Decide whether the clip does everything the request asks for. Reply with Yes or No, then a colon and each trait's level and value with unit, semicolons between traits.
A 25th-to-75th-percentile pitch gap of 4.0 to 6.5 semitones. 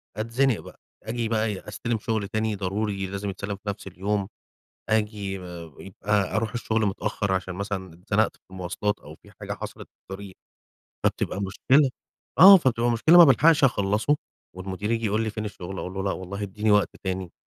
No: narrow, 2.5 semitones